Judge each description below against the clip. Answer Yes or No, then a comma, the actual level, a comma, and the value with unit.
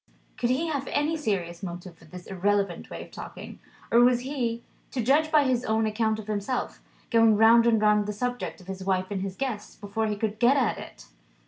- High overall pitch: Yes, high, 220 Hz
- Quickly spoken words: Yes, fast, 215 wpm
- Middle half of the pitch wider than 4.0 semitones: No, average, 3.7 semitones